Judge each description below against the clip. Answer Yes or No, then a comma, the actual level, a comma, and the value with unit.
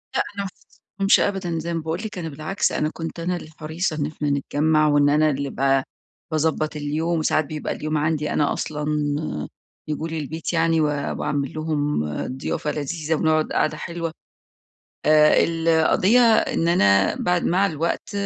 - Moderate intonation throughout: No, narrow, 1.9 semitones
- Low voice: No, medium, 155 Hz